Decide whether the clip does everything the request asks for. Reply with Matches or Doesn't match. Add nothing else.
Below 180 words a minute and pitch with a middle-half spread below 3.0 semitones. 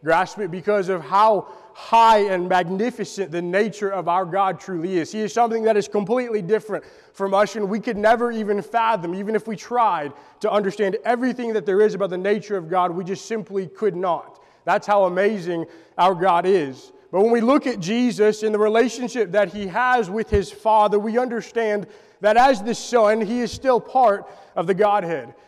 Doesn't match